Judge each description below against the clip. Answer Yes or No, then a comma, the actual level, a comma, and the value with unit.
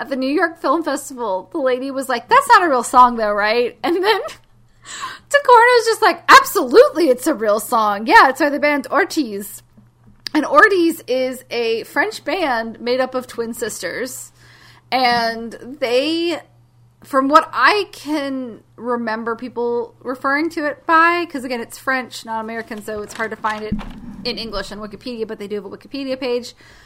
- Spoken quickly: No, average, 180 wpm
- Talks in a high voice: Yes, very high, 255 Hz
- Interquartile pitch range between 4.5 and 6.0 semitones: Yes, average, 5.2 semitones